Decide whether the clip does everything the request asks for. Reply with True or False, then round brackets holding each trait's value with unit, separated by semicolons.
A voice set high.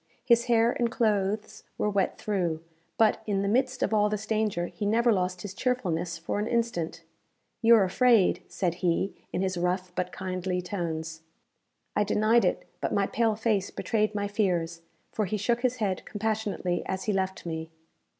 True (205 Hz)